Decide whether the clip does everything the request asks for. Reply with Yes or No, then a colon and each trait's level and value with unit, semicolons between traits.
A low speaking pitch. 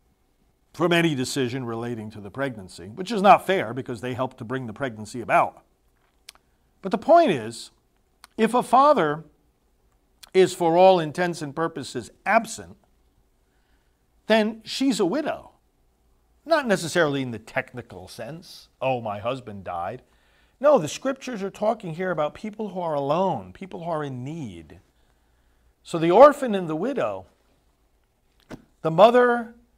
No: medium, 155 Hz